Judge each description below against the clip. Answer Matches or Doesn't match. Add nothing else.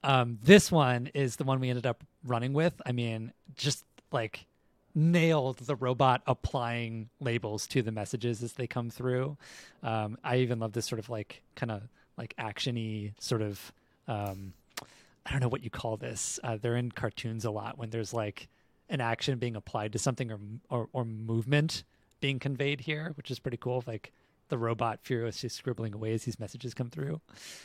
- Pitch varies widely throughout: Doesn't match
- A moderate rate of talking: Matches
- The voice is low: Matches